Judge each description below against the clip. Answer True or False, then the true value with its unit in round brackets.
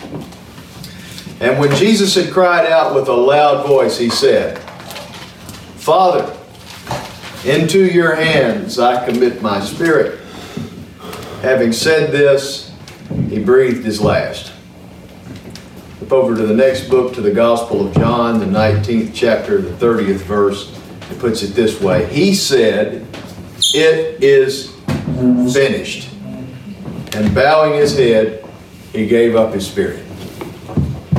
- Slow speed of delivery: True (120 wpm)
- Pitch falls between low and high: False (130 Hz)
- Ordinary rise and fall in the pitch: False (7.6 semitones)